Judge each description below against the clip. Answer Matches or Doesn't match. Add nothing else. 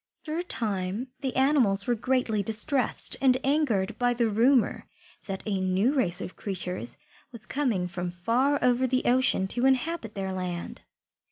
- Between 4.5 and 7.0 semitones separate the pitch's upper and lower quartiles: Matches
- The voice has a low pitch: Doesn't match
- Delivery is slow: Doesn't match